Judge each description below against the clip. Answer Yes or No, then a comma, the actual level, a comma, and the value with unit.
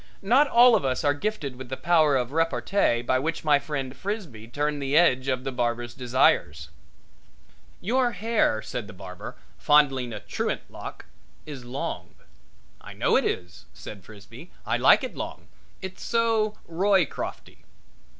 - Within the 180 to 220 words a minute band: No, average, 155 wpm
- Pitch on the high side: No, medium, 140 Hz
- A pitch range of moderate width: No, wide, 6.8 semitones